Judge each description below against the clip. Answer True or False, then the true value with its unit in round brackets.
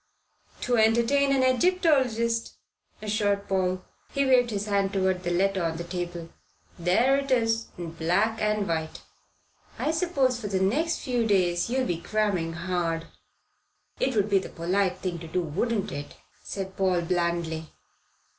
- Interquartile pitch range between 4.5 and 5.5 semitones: True (5.1 semitones)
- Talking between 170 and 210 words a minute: False (155 wpm)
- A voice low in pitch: False (195 Hz)